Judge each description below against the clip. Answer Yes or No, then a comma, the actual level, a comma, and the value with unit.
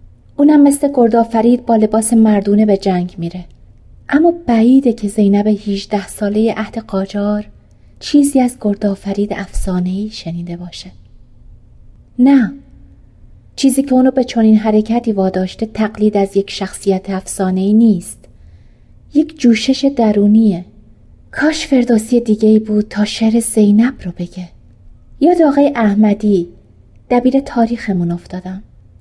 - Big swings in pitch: No, average, 4.3 semitones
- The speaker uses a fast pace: No, average, 120 wpm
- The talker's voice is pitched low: No, high, 210 Hz